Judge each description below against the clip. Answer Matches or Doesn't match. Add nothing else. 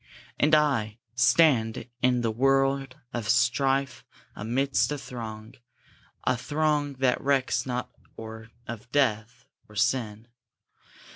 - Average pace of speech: Doesn't match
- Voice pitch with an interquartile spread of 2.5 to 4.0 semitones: Matches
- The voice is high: Doesn't match